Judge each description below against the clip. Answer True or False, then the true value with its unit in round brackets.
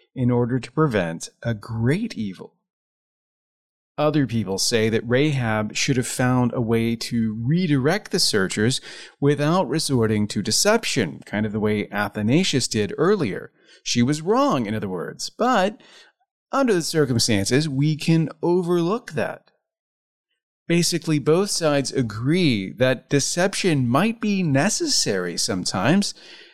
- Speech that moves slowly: True (125 wpm)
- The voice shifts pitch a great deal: True (7.0 semitones)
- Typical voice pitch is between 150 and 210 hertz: False (140 Hz)